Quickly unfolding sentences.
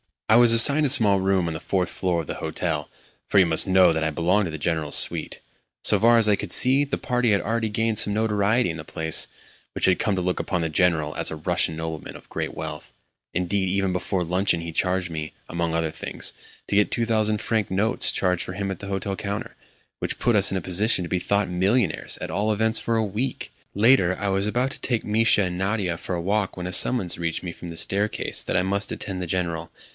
Yes: fast, 240 wpm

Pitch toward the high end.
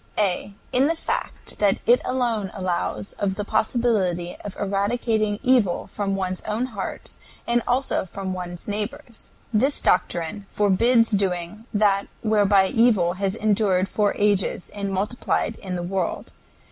Yes: high, 205 Hz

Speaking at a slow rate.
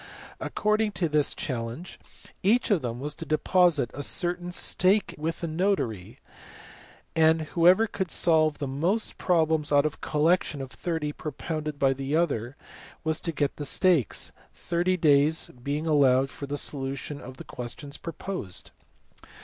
No: average, 150 wpm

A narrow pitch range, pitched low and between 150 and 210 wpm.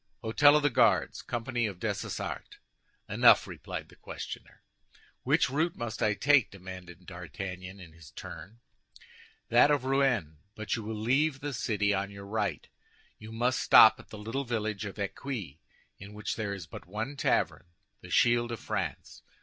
No: average, 4.1 semitones; low, 110 Hz; average, 160 wpm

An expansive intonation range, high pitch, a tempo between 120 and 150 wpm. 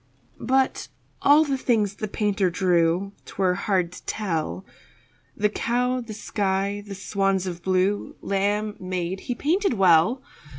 No: average, 3.2 semitones; high, 200 Hz; slow, 135 wpm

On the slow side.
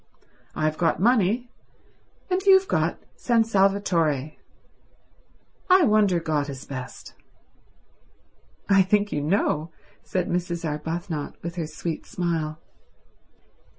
Yes: slow, 105 wpm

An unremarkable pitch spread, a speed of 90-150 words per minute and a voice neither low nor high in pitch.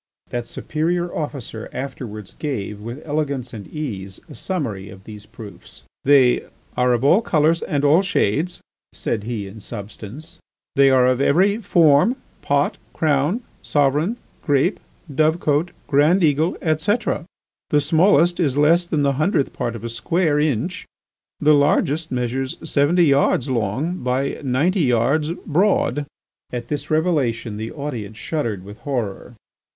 Yes: average, 4.8 semitones; average, 140 wpm; medium, 145 Hz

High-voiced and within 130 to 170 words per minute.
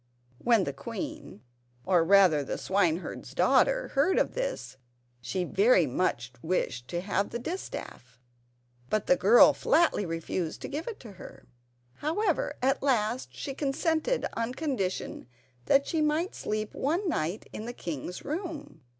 Yes: high, 220 Hz; average, 140 wpm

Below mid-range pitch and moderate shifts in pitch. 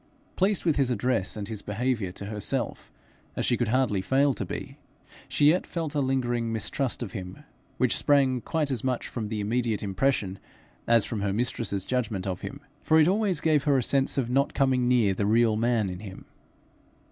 Yes: low, 120 Hz; average, 4.7 semitones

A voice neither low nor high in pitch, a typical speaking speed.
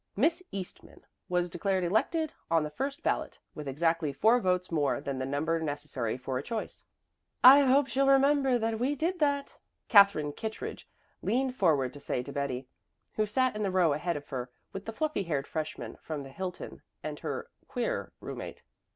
Yes: medium, 180 Hz; average, 180 wpm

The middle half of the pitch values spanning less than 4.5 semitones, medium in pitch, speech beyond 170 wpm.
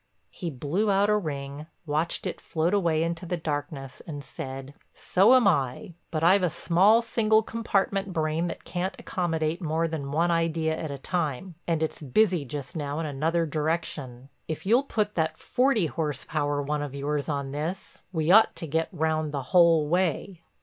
Yes: average, 3.7 semitones; medium, 160 Hz; average, 180 wpm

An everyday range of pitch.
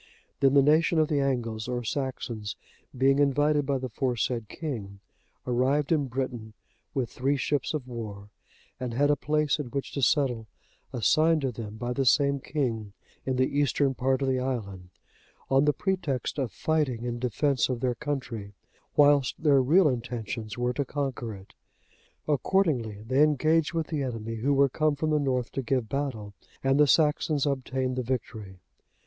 Yes: average, 3.3 semitones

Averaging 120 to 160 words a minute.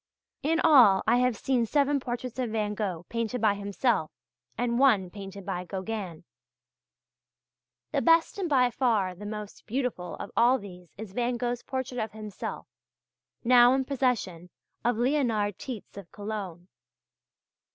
Yes: average, 150 wpm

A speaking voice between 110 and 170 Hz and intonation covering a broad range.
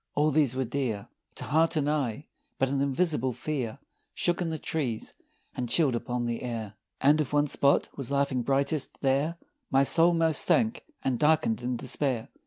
No: medium, 140 Hz; average, 3.7 semitones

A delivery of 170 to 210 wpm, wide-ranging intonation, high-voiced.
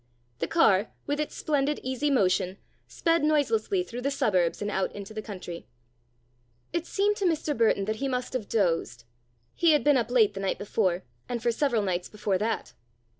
Yes: average, 185 wpm; wide, 6.7 semitones; high, 230 Hz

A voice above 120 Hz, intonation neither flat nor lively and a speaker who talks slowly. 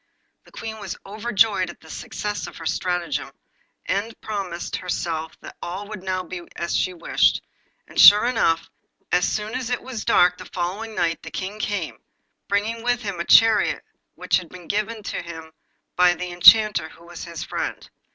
No: high, 190 Hz; average, 3.7 semitones; average, 175 wpm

